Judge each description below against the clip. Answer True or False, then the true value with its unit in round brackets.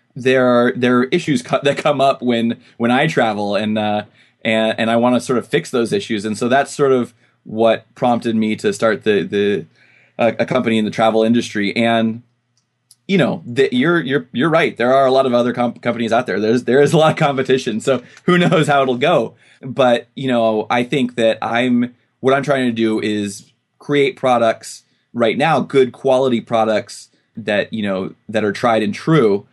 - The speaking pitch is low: True (120 Hz)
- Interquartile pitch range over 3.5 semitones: False (3.0 semitones)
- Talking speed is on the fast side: True (210 wpm)